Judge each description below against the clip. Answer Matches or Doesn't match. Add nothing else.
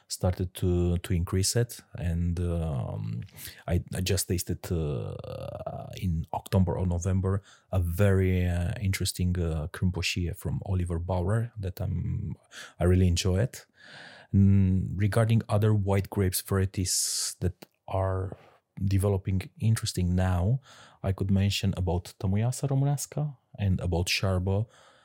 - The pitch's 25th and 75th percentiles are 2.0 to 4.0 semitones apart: Matches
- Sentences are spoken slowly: Matches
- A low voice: Matches